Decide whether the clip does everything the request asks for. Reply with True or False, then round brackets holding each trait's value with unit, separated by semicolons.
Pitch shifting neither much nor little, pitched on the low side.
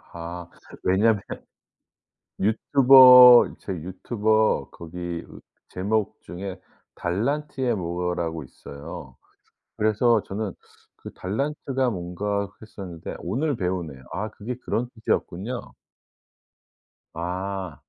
True (4.9 semitones; 100 Hz)